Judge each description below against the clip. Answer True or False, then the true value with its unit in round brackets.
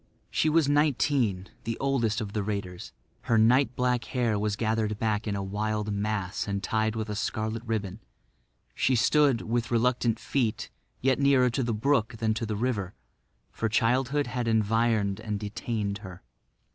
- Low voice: True (110 Hz)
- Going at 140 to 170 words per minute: True (160 wpm)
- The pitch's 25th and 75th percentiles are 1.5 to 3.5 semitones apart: True (2.9 semitones)